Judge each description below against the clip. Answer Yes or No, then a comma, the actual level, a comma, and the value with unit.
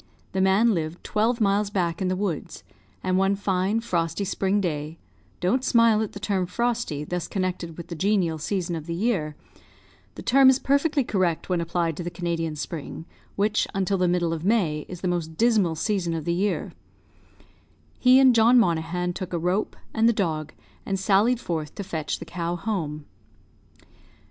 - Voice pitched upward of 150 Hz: Yes, medium, 185 Hz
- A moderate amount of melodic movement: Yes, average, 4.0 semitones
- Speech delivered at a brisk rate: No, average, 180 wpm